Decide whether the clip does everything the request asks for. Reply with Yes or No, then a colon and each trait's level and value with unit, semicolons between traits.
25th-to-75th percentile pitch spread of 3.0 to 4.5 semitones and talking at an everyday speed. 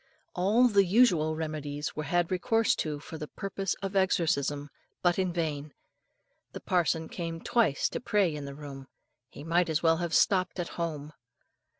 Yes: average, 3.6 semitones; average, 170 wpm